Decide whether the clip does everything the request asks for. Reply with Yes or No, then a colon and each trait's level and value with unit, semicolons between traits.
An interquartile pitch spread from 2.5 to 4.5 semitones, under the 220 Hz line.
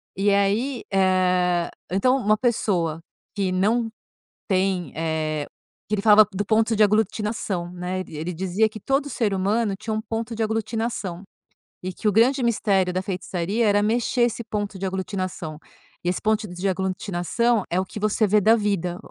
Yes: average, 3.2 semitones; high, 200 Hz